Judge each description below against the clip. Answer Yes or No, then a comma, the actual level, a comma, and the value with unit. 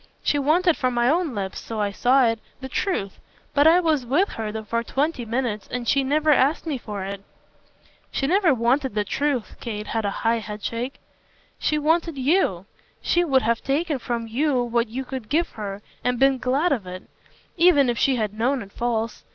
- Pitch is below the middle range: No, very high, 255 Hz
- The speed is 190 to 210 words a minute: Yes, average, 195 wpm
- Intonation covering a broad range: No, average, 4.5 semitones